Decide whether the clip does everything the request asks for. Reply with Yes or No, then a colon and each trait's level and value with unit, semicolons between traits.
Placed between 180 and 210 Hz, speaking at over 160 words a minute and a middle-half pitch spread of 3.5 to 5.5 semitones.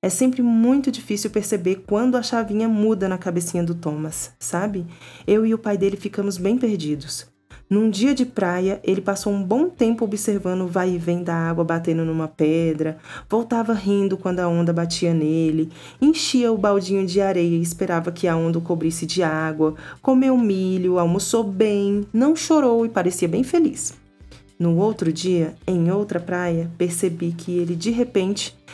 Yes: high, 190 Hz; average, 175 wpm; average, 4.3 semitones